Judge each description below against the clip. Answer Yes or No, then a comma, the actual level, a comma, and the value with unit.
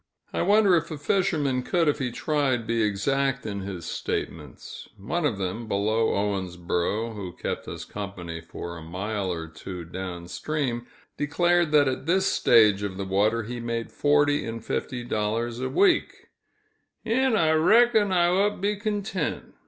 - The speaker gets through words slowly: No, average, 165 wpm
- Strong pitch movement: Yes, wide, 8.3 semitones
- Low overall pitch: Yes, low, 120 Hz